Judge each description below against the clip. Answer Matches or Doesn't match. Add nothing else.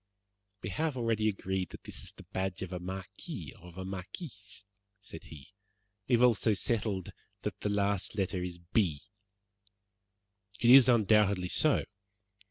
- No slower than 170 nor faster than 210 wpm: Doesn't match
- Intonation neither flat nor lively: Matches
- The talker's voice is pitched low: Matches